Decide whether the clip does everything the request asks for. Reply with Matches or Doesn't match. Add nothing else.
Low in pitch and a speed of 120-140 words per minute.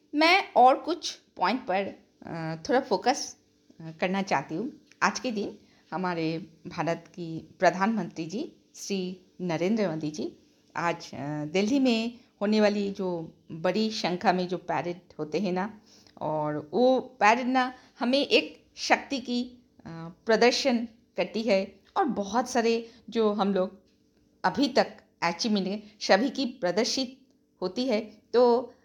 Doesn't match